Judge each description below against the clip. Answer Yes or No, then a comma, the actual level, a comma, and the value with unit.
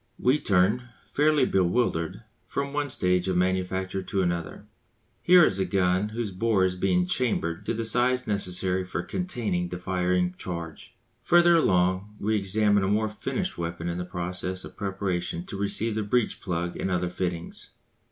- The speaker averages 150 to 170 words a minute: Yes, average, 160 wpm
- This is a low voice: Yes, very low, 95 Hz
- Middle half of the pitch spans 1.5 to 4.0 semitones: Yes, average, 3.4 semitones